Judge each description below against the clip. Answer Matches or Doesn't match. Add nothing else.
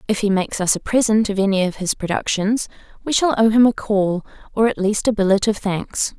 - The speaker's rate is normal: Doesn't match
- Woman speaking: Matches